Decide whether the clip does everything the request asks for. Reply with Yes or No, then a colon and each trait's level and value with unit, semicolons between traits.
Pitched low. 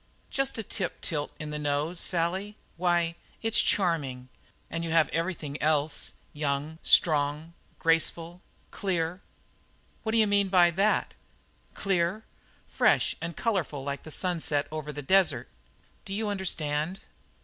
No: medium, 165 Hz